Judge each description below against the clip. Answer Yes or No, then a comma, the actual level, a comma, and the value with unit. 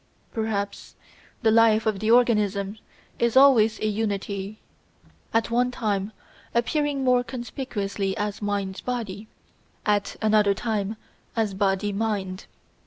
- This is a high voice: Yes, high, 215 Hz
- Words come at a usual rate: No, slow, 115 wpm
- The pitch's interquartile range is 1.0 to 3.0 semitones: Yes, narrow, 2.5 semitones